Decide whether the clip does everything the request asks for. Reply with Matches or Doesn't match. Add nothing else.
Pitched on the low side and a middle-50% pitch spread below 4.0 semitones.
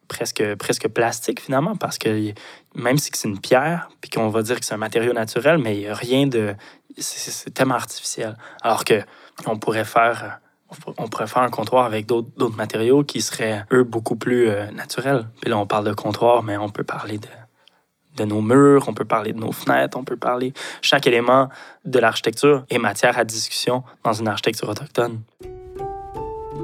Matches